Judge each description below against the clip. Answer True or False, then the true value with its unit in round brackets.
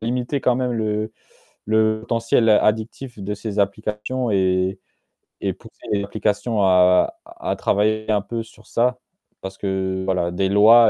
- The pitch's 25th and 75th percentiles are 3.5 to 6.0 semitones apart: False (2.9 semitones)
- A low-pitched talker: True (105 Hz)